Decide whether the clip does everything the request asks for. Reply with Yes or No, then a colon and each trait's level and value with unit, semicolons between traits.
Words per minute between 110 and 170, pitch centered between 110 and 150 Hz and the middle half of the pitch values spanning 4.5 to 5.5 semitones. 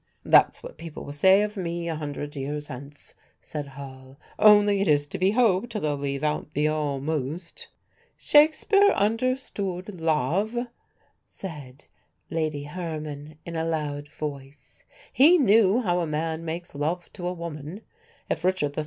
No: average, 150 wpm; medium, 160 Hz; average, 4.8 semitones